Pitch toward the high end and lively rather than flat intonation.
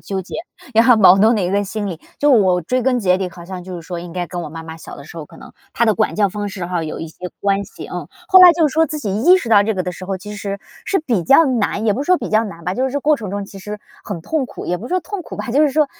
Yes: high, 205 Hz; wide, 5.9 semitones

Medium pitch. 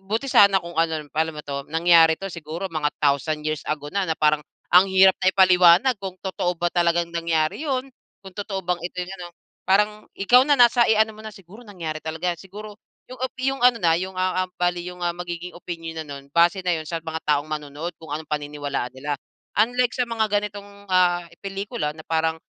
Yes: medium, 175 Hz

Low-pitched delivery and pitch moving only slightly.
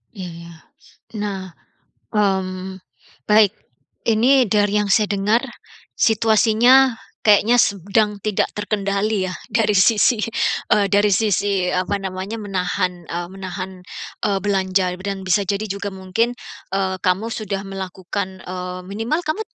No: high, 200 Hz; narrow, 2.3 semitones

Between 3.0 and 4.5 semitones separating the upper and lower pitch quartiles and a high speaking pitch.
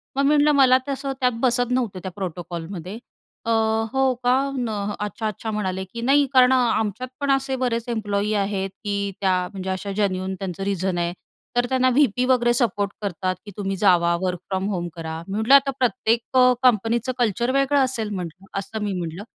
No: average, 4.9 semitones; high, 210 Hz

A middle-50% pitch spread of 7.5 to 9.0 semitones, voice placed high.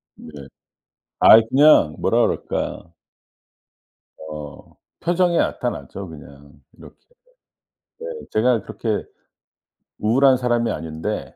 No: wide, 8.3 semitones; low, 110 Hz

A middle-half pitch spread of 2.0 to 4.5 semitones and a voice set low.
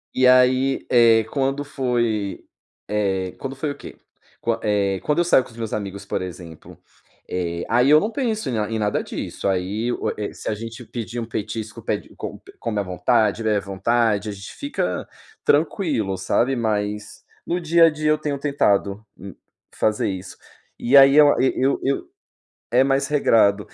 No: average, 4.9 semitones; low, 115 Hz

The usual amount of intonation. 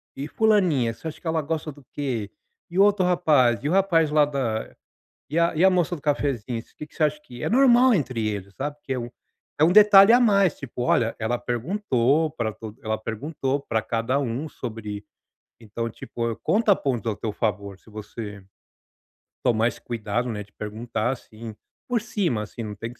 No: wide, 6.4 semitones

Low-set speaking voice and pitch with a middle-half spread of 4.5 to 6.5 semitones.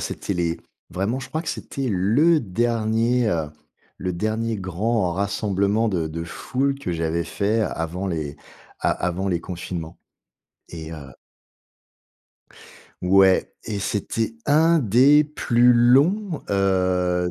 Yes: low, 100 Hz; average, 5.2 semitones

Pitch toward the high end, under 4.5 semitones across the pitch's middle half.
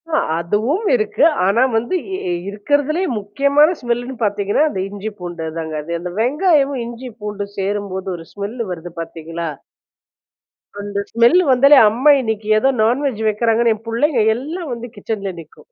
No: high, 225 Hz; average, 5.3 semitones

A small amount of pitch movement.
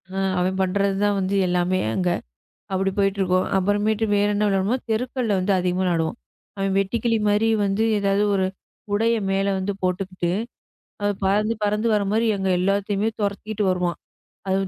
Yes: narrow, 1.8 semitones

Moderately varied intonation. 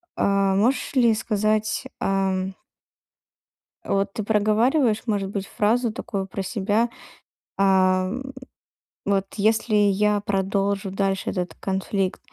No: narrow, 2.0 semitones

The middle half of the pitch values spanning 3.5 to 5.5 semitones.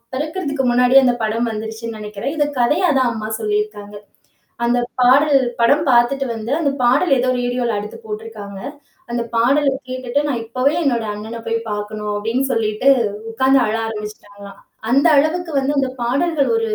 Yes: average, 4.1 semitones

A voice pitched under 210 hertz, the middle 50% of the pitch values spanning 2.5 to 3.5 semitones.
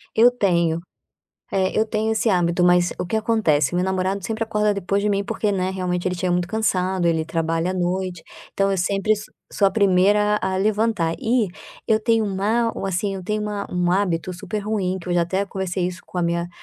Yes: high, 190 Hz; average, 2.9 semitones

